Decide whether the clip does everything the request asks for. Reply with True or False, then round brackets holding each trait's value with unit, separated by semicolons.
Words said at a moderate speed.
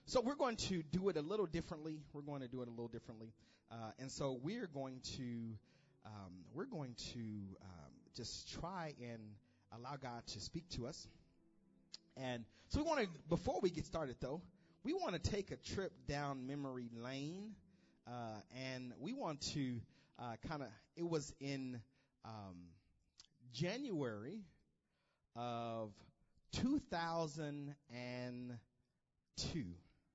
True (145 wpm)